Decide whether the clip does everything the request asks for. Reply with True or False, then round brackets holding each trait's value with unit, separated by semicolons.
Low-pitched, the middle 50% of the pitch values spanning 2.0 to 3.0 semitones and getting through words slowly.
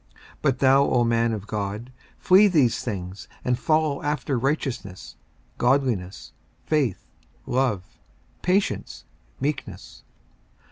False (125 Hz; 5.1 semitones; 105 wpm)